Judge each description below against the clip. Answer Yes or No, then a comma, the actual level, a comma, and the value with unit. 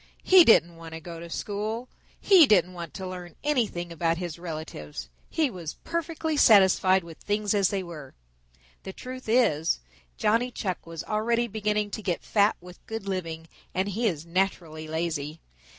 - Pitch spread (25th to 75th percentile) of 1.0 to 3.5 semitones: No, average, 4.6 semitones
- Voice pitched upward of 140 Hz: Yes, medium, 185 Hz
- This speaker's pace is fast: No, average, 165 wpm